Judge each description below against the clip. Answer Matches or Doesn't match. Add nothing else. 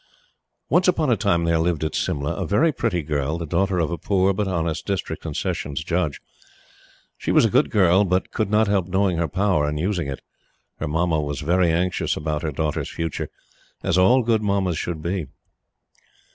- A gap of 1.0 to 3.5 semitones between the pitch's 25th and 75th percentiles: Doesn't match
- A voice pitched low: Matches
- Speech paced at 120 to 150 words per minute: Doesn't match